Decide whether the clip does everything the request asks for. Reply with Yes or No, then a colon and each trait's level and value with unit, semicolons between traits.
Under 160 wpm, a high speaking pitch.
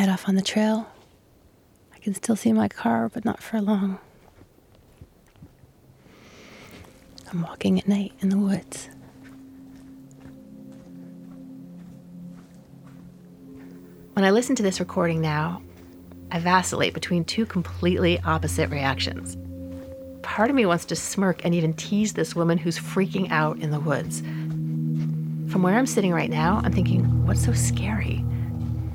No: slow, 135 wpm; low, 135 Hz